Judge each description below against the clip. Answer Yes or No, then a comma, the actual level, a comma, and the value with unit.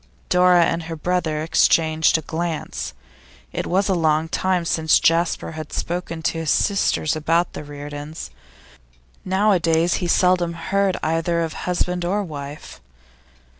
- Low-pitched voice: No, medium, 165 Hz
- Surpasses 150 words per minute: No, slow, 135 wpm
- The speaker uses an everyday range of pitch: No, narrow, 2.2 semitones